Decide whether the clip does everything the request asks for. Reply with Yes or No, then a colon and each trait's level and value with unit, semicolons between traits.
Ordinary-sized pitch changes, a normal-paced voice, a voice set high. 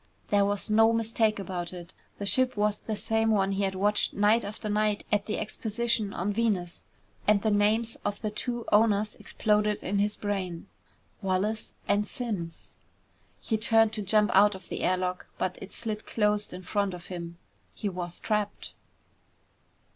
No: narrow, 2.0 semitones; average, 170 wpm; high, 210 Hz